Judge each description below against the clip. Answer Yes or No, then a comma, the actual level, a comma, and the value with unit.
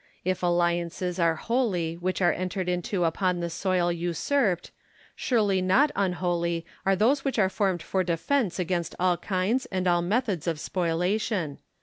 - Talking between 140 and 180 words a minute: Yes, average, 150 wpm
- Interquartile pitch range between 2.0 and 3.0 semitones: Yes, narrow, 2.4 semitones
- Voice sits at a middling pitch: Yes, medium, 180 Hz